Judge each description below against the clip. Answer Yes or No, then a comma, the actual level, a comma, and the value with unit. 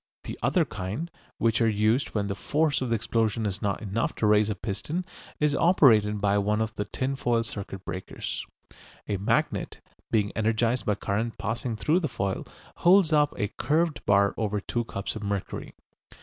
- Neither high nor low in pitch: No, low, 110 Hz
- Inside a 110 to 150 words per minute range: No, average, 180 wpm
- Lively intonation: No, average, 3.8 semitones